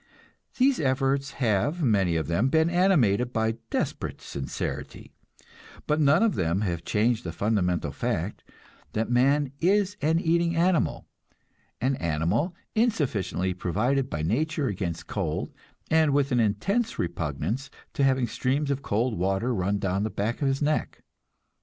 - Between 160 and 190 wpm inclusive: No, average, 140 wpm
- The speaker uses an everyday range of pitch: No, wide, 7.6 semitones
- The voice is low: Yes, low, 125 Hz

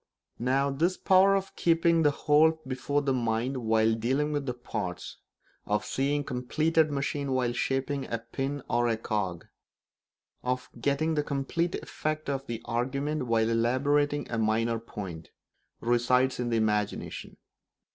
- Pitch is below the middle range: Yes, low, 130 Hz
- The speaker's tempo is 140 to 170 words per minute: Yes, average, 145 wpm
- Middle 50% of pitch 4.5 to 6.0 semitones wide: No, average, 4.0 semitones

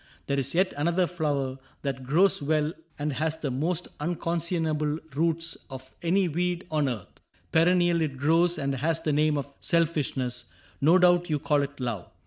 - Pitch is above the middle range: No, medium, 155 Hz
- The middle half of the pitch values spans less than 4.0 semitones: Yes, average, 3.3 semitones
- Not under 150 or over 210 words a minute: Yes, average, 165 wpm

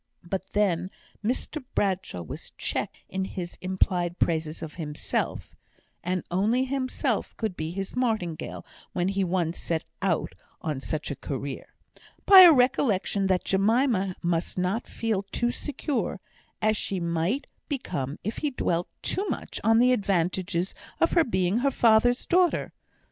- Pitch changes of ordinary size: No, wide, 5.7 semitones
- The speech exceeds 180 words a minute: No, average, 145 wpm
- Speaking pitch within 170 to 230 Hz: Yes, high, 190 Hz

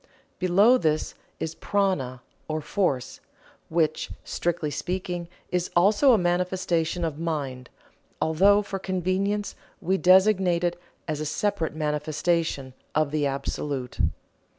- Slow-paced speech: Yes, slow, 115 wpm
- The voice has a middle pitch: Yes, medium, 170 Hz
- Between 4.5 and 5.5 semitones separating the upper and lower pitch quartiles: No, average, 3.6 semitones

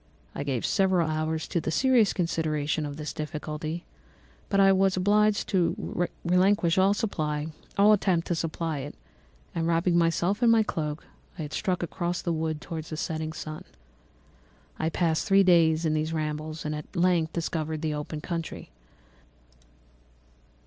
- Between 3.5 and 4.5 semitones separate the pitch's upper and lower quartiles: No, average, 2.8 semitones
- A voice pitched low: No, medium, 165 Hz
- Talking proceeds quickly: No, average, 150 wpm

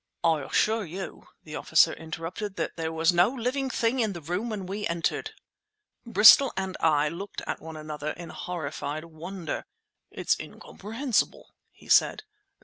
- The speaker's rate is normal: Yes, average, 150 wpm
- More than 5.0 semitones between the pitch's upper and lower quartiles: No, average, 4.7 semitones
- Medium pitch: Yes, medium, 180 Hz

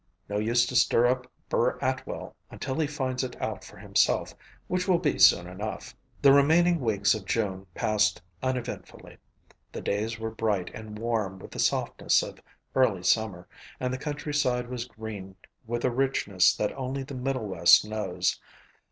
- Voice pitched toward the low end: Yes, low, 115 Hz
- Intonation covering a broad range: No, average, 4.2 semitones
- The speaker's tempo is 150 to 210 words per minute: Yes, average, 165 wpm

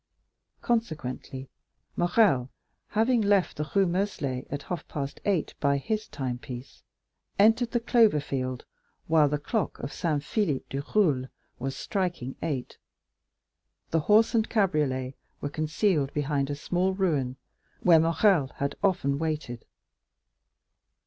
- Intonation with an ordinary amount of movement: No, wide, 6.3 semitones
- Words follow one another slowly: Yes, slow, 125 wpm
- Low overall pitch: No, medium, 155 Hz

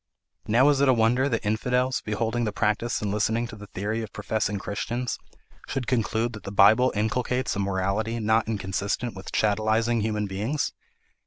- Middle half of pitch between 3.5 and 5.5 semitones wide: No, narrow, 2.5 semitones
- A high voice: No, low, 110 Hz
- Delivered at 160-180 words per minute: Yes, average, 170 wpm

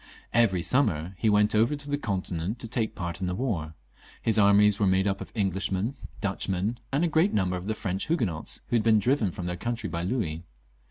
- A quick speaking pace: Yes, fast, 215 wpm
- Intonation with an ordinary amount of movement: Yes, average, 4.1 semitones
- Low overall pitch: Yes, low, 100 Hz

